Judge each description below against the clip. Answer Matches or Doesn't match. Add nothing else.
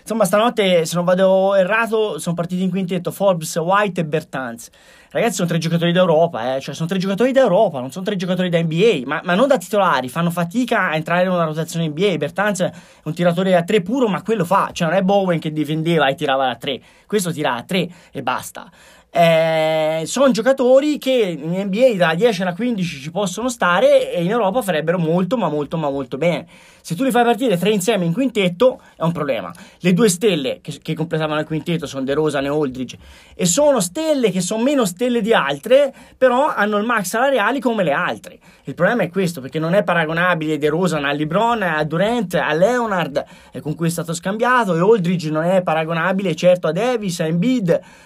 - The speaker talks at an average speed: Doesn't match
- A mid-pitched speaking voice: Matches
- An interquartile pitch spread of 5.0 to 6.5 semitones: Matches